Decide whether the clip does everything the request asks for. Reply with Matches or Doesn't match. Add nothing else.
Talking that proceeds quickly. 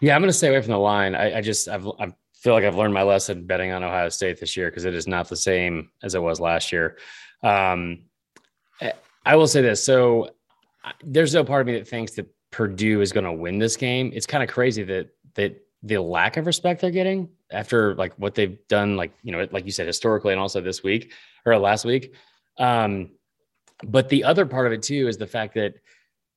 Matches